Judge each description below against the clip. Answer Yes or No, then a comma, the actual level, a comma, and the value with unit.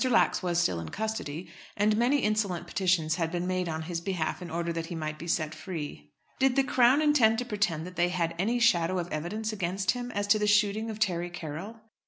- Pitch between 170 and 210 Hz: Yes, medium, 185 Hz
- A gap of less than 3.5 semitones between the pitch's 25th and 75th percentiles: No, average, 4.5 semitones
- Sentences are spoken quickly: Yes, fast, 225 wpm